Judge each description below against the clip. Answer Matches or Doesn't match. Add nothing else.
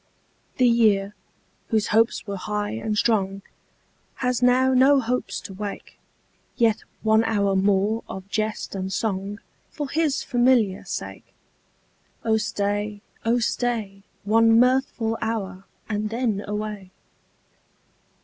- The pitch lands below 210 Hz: Doesn't match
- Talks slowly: Matches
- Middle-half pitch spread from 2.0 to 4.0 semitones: Matches